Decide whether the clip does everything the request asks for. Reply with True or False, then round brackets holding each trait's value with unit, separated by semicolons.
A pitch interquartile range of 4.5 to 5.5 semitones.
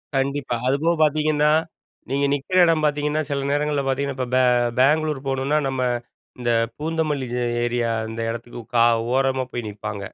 False (2.7 semitones)